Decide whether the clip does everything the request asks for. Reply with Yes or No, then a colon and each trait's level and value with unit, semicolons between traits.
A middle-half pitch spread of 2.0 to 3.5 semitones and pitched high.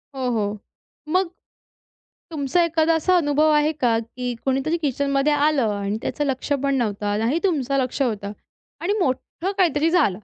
No: average, 4.7 semitones; very high, 275 Hz